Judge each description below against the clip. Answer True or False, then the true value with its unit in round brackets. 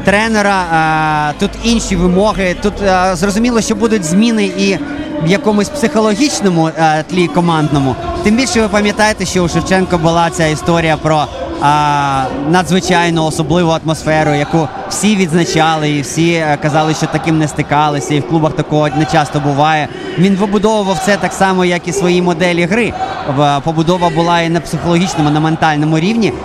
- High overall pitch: False (175 Hz)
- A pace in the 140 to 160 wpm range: True (145 wpm)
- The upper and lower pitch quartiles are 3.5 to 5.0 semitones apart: True (4.1 semitones)